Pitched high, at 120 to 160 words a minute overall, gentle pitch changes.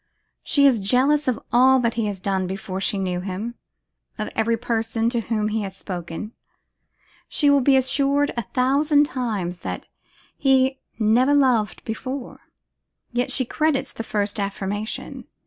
No: high, 230 Hz; average, 150 wpm; average, 4.5 semitones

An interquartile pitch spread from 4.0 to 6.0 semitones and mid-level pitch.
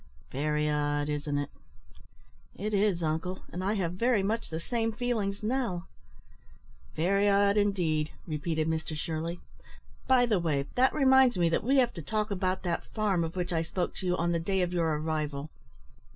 Yes: average, 4.8 semitones; medium, 180 Hz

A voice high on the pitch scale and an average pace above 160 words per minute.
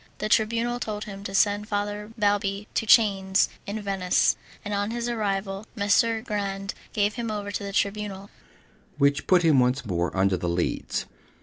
Yes: high, 205 Hz; average, 170 wpm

